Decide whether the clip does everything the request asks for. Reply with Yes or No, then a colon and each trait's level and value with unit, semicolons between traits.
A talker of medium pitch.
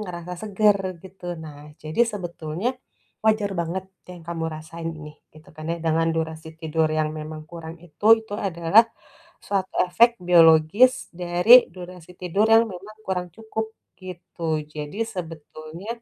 Yes: medium, 175 Hz